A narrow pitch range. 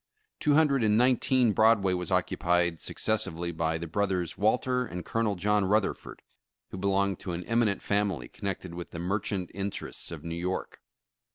No: average, 3.7 semitones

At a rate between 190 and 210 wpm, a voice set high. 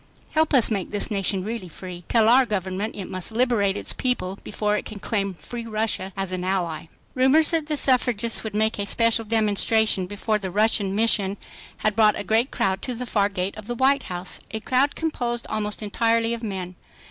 Yes: average, 200 wpm; high, 215 Hz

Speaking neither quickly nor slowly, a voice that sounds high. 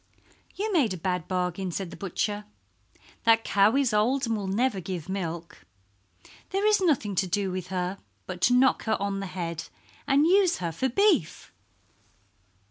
Yes: average, 170 wpm; high, 200 Hz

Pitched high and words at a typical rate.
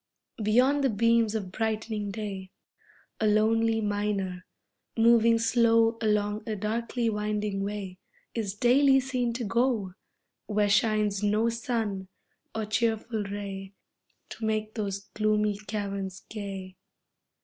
No: high, 215 Hz; slow, 115 wpm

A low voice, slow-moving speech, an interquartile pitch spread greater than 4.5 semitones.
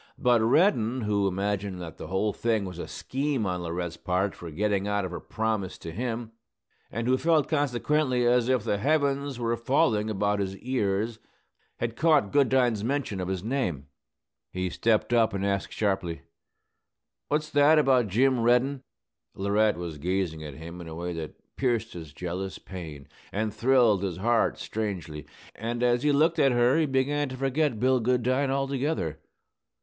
No: low, 110 Hz; average, 170 wpm; wide, 5.5 semitones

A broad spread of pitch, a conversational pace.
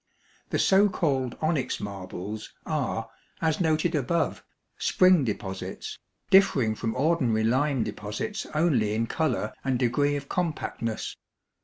No: wide, 6.4 semitones; slow, 120 wpm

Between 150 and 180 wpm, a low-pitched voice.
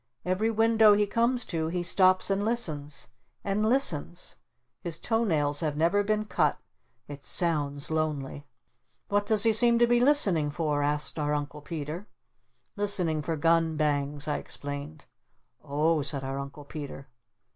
No: average, 155 wpm; medium, 160 Hz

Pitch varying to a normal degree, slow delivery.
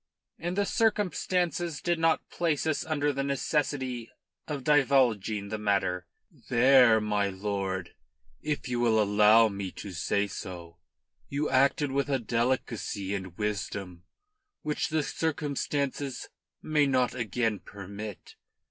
No: wide, 6.2 semitones; slow, 125 wpm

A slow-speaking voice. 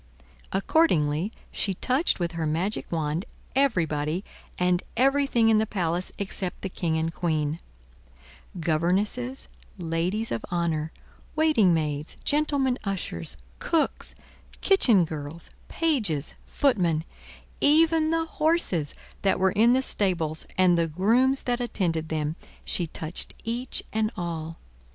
Yes: slow, 120 wpm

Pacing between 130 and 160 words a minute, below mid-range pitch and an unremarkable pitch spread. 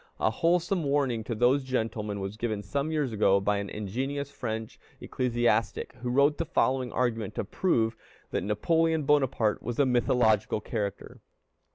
Yes: average, 155 wpm; low, 120 Hz; average, 4.6 semitones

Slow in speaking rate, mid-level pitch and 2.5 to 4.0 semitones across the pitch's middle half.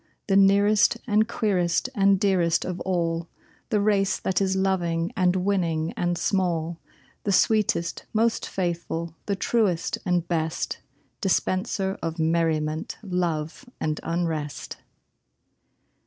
Yes: slow, 115 wpm; medium, 180 Hz; average, 2.9 semitones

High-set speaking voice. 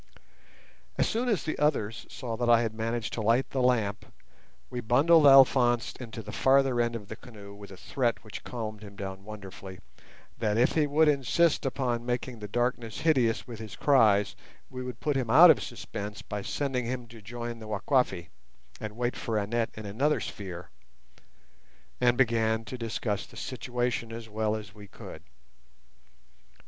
No: low, 115 Hz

